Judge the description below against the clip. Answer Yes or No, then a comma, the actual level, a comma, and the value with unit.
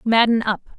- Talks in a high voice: Yes, high, 225 Hz